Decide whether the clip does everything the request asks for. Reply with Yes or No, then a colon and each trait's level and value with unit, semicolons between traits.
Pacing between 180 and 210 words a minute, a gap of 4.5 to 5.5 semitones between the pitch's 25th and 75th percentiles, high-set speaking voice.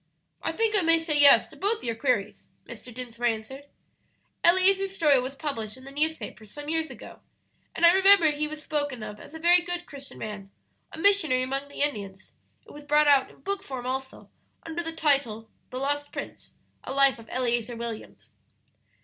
Yes: average, 190 wpm; average, 4.8 semitones; very high, 285 Hz